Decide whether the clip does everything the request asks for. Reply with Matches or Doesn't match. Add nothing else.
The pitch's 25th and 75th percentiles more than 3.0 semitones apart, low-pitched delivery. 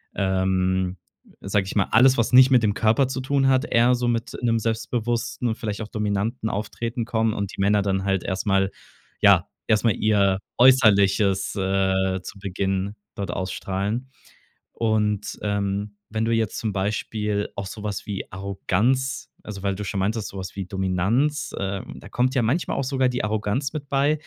Matches